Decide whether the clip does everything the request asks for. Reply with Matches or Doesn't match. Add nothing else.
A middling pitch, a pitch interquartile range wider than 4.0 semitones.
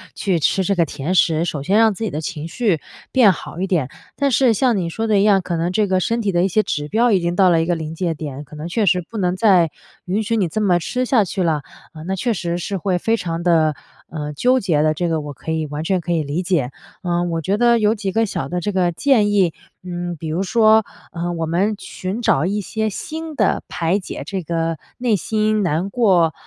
Matches